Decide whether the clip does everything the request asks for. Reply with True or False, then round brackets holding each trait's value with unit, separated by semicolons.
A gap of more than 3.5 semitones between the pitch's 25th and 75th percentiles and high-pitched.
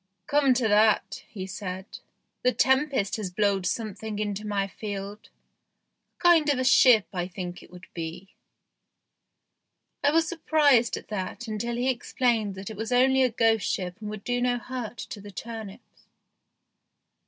True (4.1 semitones; 220 Hz)